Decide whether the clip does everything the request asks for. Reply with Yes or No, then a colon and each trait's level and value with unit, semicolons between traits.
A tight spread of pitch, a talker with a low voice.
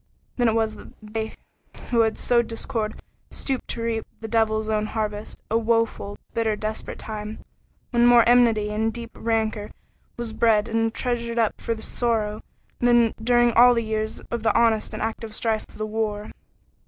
No: narrow, 1.3 semitones; high, 225 Hz